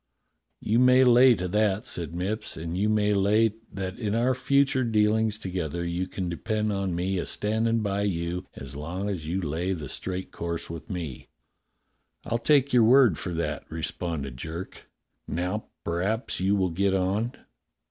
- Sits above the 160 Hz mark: No, very low, 95 Hz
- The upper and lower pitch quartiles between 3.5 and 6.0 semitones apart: Yes, average, 4.2 semitones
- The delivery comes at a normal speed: Yes, average, 170 wpm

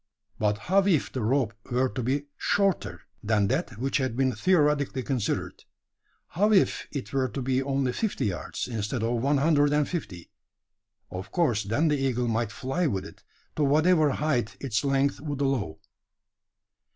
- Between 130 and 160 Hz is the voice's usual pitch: Yes, low, 135 Hz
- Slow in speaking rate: No, average, 165 wpm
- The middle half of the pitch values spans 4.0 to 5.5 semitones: Yes, average, 4.3 semitones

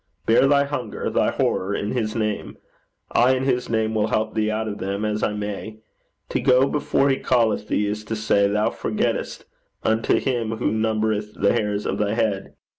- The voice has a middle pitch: No, low, 110 Hz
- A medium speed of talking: Yes, average, 190 wpm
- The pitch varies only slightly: Yes, narrow, 1.9 semitones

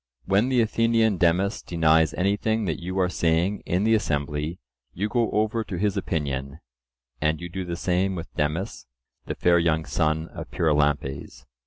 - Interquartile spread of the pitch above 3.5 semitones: Yes, average, 4.5 semitones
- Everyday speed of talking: Yes, average, 165 wpm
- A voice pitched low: Yes, very low, 90 Hz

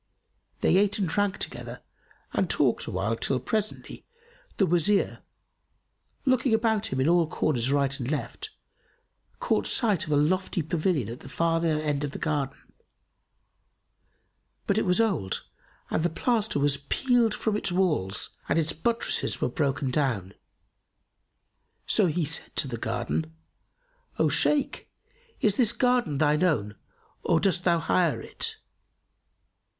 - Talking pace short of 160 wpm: Yes, average, 140 wpm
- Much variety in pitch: Yes, wide, 6.4 semitones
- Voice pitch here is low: No, medium, 165 Hz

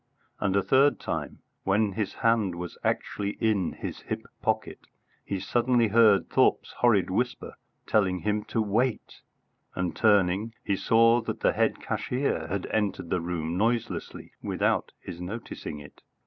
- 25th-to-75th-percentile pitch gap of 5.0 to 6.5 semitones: No, average, 3.8 semitones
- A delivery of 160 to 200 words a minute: No, average, 150 wpm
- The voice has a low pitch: Yes, low, 105 Hz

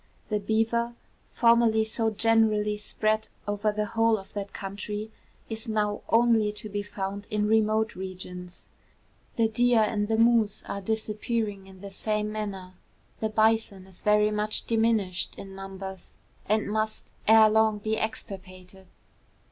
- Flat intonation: Yes, narrow, 1.8 semitones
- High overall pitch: Yes, high, 215 Hz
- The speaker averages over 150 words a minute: No, average, 140 wpm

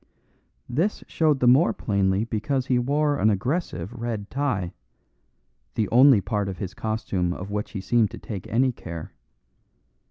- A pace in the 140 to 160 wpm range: Yes, average, 155 wpm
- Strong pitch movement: No, average, 5.0 semitones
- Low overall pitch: Yes, low, 110 Hz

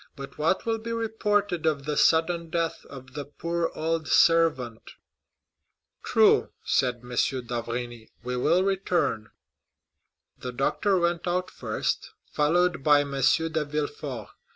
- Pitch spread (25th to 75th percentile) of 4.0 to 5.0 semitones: Yes, average, 4.6 semitones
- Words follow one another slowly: Yes, slow, 130 wpm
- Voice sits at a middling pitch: Yes, medium, 155 Hz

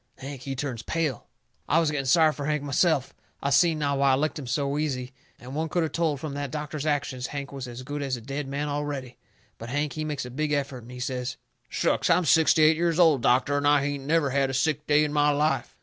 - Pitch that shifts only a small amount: Yes, narrow, 2.3 semitones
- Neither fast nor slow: No, fast, 250 wpm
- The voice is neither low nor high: Yes, medium, 145 Hz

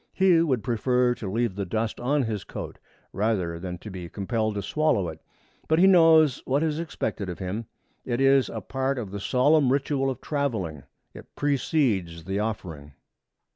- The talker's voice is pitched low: Yes, low, 115 Hz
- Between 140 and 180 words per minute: Yes, average, 175 wpm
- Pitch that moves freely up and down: Yes, wide, 6.2 semitones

